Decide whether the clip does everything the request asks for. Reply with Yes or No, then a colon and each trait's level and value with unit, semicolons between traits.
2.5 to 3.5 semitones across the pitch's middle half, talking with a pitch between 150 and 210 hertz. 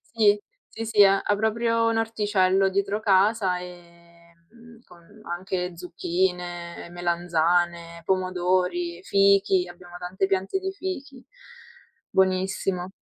Yes: average, 2.8 semitones; medium, 185 Hz